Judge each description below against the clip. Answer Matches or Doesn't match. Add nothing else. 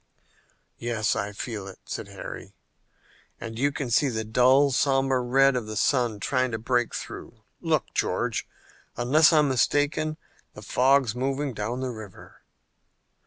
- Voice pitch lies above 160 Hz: Doesn't match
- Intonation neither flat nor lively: Matches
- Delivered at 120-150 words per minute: Matches